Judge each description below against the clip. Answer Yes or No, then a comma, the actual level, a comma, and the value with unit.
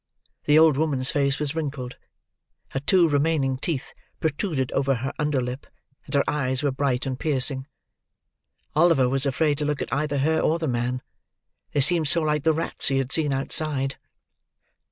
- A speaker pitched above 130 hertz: Yes, medium, 140 Hz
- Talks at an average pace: Yes, average, 175 wpm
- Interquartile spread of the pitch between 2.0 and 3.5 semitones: Yes, narrow, 2.5 semitones